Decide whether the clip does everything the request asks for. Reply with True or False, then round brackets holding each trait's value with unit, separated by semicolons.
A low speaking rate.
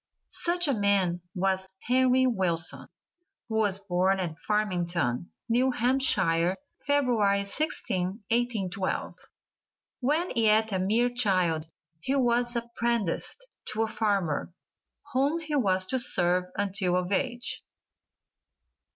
True (110 wpm)